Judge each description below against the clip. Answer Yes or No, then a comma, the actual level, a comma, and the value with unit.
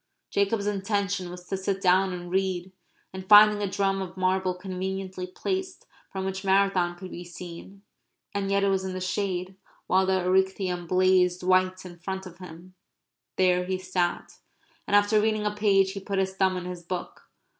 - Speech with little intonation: Yes, narrow, 1.3 semitones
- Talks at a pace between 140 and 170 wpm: No, average, 180 wpm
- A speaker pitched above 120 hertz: Yes, high, 190 Hz